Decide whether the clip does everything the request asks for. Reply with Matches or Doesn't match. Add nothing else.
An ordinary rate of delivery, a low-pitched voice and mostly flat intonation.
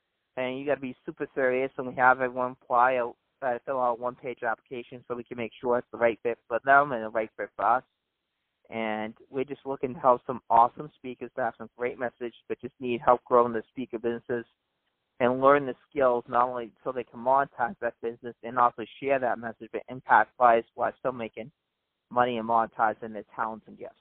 Doesn't match